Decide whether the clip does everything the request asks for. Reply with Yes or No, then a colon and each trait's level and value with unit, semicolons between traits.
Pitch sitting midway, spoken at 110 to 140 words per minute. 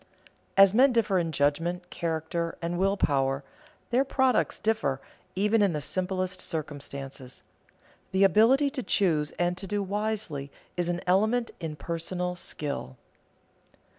Yes: medium, 180 Hz; slow, 135 wpm